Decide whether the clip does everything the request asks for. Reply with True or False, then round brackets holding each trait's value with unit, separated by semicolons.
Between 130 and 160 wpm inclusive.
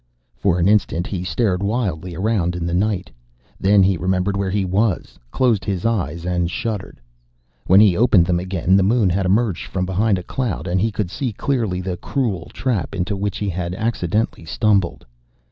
False (185 wpm)